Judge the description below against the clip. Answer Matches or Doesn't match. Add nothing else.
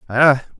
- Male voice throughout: Matches